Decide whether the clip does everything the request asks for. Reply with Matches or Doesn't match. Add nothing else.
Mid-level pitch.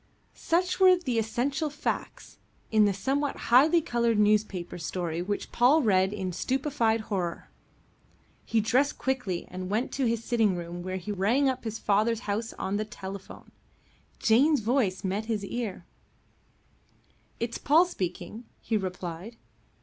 Doesn't match